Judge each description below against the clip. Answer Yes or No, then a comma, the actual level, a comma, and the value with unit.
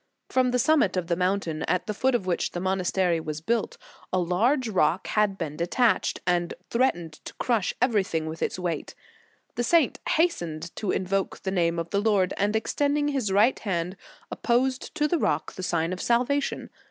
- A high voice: Yes, high, 195 Hz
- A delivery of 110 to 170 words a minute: No, average, 190 wpm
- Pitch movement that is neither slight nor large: No, wide, 5.8 semitones